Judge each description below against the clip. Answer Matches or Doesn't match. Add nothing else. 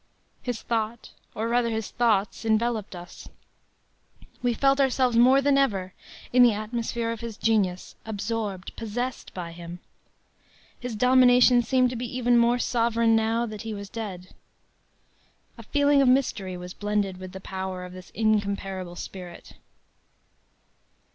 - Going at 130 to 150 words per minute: Matches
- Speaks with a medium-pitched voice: Doesn't match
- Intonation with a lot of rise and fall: Doesn't match